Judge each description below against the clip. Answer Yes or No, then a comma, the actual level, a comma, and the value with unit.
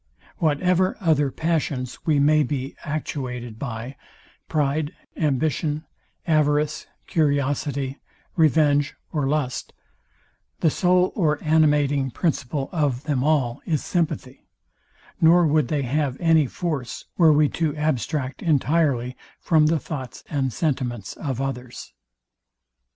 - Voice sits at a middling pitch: Yes, medium, 150 Hz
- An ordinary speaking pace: No, slow, 110 wpm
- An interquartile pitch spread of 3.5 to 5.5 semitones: No, average, 2.8 semitones